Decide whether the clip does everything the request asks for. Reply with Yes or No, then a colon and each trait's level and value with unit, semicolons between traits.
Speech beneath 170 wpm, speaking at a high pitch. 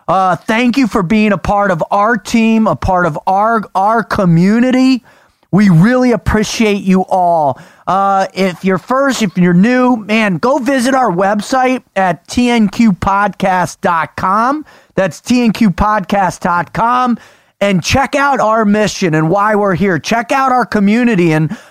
Yes: average, 140 wpm; high, 210 Hz